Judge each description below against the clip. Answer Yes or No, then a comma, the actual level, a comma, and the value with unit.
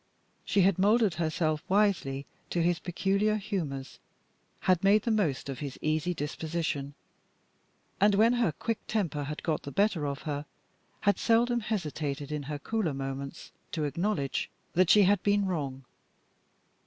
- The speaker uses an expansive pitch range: Yes, wide, 5.8 semitones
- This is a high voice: No, medium, 170 Hz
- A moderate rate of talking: Yes, average, 150 wpm